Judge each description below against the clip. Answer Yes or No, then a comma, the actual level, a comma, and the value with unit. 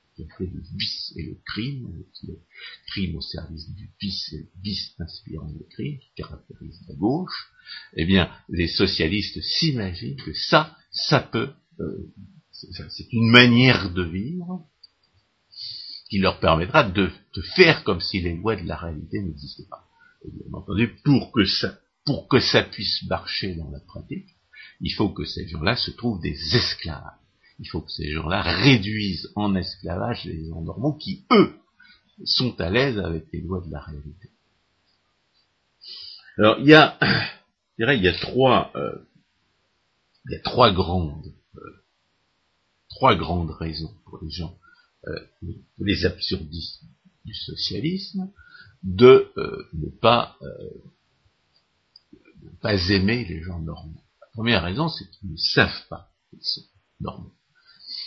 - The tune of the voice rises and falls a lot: Yes, wide, 5.9 semitones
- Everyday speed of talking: Yes, average, 155 wpm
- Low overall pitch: Yes, very low, 95 Hz